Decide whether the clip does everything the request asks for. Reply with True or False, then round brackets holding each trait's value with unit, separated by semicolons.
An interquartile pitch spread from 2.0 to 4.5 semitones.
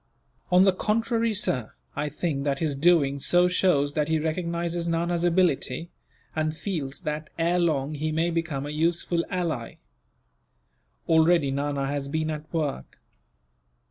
True (3.2 semitones)